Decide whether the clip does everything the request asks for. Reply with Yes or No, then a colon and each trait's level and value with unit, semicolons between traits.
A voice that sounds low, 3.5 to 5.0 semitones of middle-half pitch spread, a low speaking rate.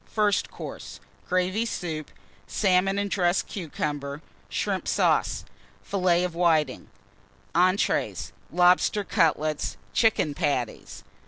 No: medium, 180 Hz; average, 4.0 semitones; slow, 95 wpm